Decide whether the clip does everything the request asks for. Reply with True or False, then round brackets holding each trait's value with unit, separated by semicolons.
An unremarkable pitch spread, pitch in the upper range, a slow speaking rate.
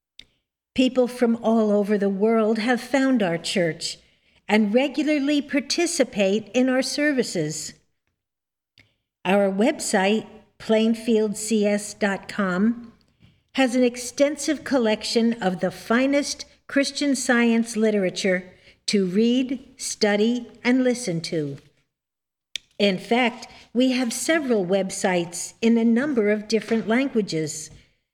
True (4.3 semitones; 220 Hz; 100 wpm)